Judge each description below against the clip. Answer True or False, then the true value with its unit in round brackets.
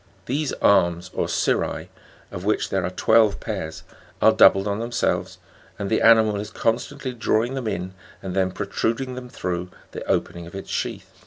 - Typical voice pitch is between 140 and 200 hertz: False (105 Hz)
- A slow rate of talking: False (175 wpm)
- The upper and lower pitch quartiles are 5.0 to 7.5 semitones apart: False (3.7 semitones)